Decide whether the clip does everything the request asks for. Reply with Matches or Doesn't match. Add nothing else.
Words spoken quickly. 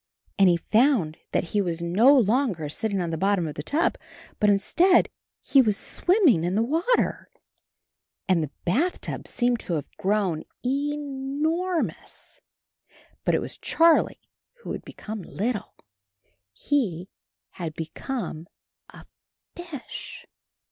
Doesn't match